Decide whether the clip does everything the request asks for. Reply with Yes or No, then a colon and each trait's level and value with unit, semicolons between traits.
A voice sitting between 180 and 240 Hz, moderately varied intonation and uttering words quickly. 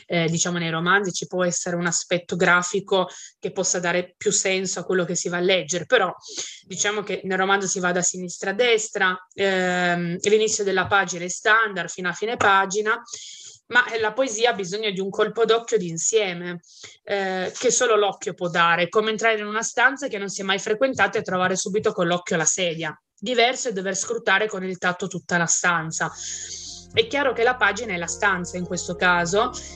Yes: high, 190 Hz; average, 3.3 semitones; fast, 200 wpm